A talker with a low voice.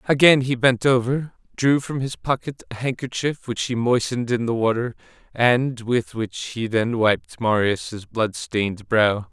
Yes: low, 120 Hz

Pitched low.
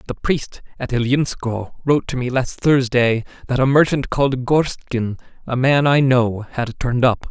Yes: low, 130 Hz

